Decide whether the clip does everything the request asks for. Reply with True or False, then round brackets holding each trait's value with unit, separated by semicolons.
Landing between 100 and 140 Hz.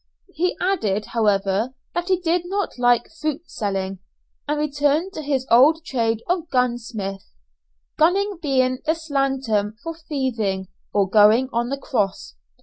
False (260 Hz)